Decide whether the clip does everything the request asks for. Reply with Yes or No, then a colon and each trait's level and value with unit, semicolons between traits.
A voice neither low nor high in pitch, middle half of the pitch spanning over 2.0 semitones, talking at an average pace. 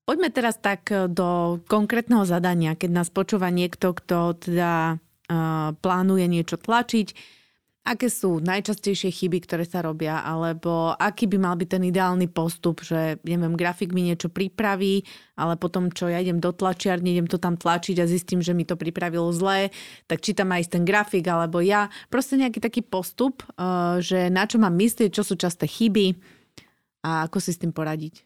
No: medium, 180 Hz; narrow, 2.6 semitones; fast, 180 wpm